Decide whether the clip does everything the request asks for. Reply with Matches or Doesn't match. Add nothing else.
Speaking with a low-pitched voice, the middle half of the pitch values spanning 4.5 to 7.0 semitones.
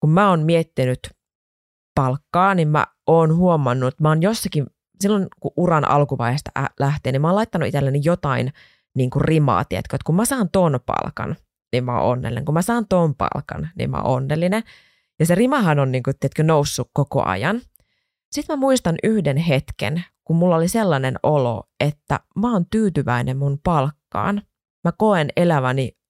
Doesn't match